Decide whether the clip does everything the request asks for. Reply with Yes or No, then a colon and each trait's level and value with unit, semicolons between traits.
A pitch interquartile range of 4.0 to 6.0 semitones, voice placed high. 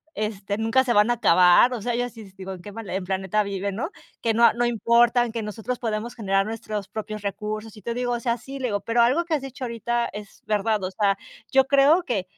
No: average, 2.8 semitones; high, 225 Hz